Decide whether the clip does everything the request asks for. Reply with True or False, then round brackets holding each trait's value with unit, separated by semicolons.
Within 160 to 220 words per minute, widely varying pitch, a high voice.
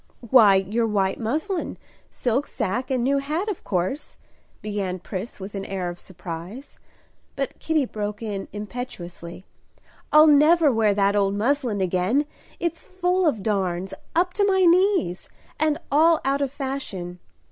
False (145 wpm; 7.5 semitones; 230 Hz)